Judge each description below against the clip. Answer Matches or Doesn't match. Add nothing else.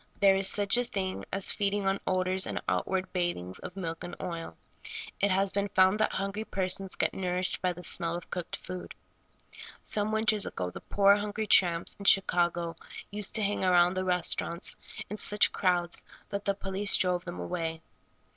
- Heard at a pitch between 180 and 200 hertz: Matches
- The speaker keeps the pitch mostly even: Matches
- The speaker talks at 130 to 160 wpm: Doesn't match